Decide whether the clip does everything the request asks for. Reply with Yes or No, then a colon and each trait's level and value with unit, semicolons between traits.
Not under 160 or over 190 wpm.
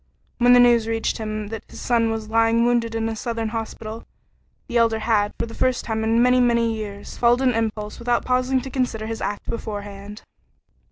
No: average, 200 wpm